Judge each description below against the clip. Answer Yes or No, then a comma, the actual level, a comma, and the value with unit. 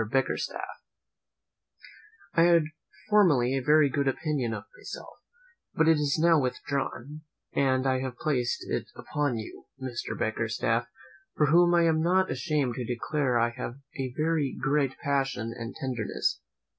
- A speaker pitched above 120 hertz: Yes, low, 135 Hz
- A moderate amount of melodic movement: Yes, average, 3.8 semitones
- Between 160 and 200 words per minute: No, average, 145 wpm